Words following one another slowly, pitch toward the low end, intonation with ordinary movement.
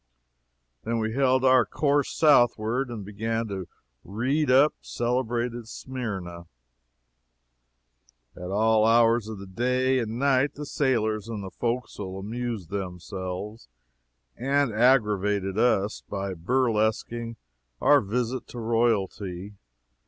Yes: slow, 110 wpm; low, 115 Hz; average, 3.8 semitones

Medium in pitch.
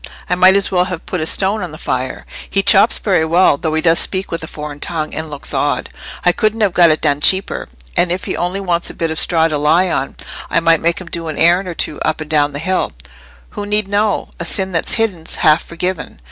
Yes: medium, 170 Hz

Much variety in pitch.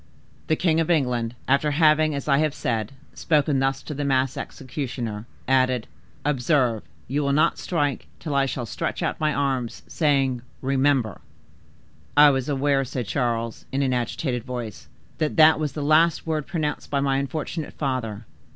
No: average, 3.1 semitones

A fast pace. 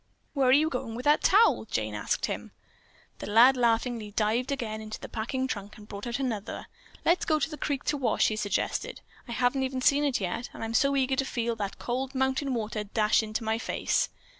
Yes: fast, 220 wpm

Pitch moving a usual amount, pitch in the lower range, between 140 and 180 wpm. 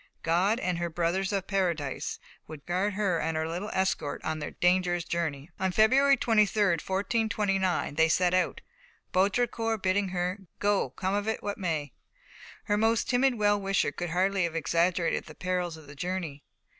No: average, 3.3 semitones; medium, 185 Hz; average, 170 wpm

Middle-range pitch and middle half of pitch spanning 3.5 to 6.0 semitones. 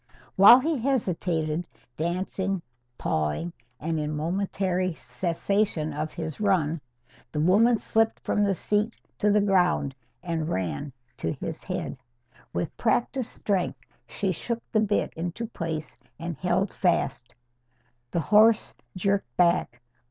Yes: medium, 180 Hz; average, 4.5 semitones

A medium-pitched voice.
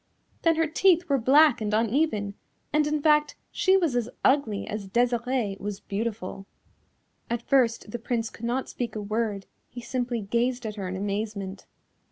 No: high, 235 Hz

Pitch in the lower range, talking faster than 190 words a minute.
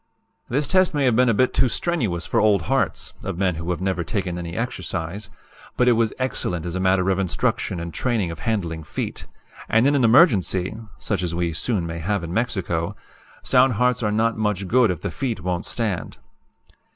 Yes: low, 100 Hz; average, 200 wpm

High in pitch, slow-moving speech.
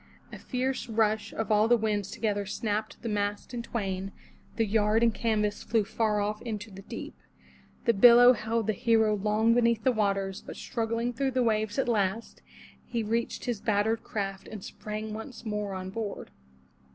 No: high, 220 Hz; average, 175 wpm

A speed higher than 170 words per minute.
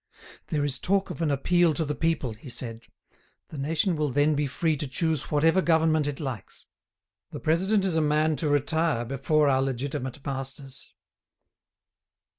No: average, 165 wpm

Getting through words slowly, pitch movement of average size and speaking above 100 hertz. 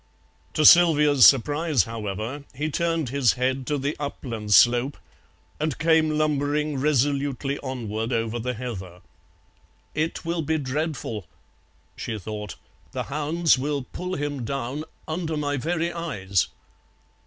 Yes: slow, 125 wpm; average, 4.3 semitones; medium, 140 Hz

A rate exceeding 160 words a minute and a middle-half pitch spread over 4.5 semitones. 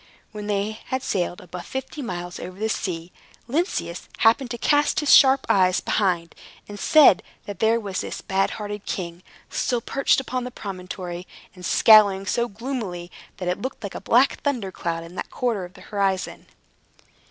Yes: average, 175 wpm; average, 5.0 semitones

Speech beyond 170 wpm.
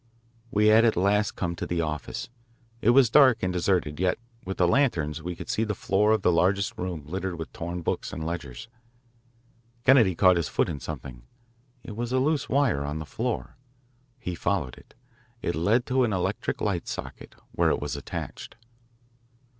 Yes: average, 185 wpm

